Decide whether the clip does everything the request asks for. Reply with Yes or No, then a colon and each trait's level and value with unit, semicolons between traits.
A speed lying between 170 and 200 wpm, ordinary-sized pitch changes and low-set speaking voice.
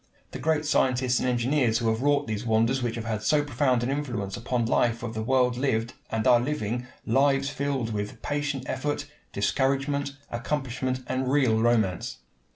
Yes: average, 175 wpm; average, 3.3 semitones; low, 125 Hz